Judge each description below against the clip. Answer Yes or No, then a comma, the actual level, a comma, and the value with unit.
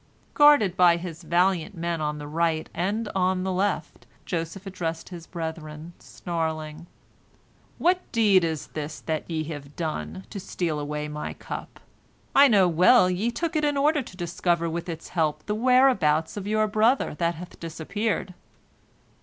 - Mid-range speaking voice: Yes, medium, 175 Hz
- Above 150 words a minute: Yes, average, 160 wpm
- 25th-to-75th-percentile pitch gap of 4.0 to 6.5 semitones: Yes, average, 4.3 semitones